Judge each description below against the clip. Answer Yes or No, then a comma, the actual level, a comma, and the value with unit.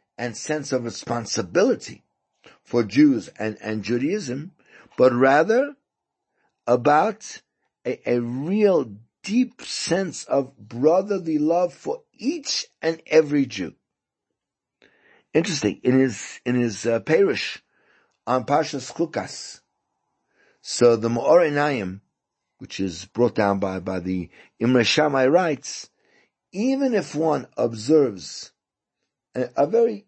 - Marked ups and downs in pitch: Yes, wide, 7.9 semitones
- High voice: No, medium, 140 Hz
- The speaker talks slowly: Yes, slow, 110 wpm